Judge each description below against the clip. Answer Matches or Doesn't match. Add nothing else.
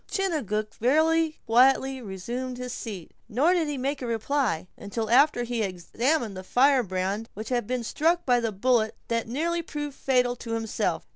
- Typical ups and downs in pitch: Matches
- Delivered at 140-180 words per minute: Matches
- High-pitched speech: Matches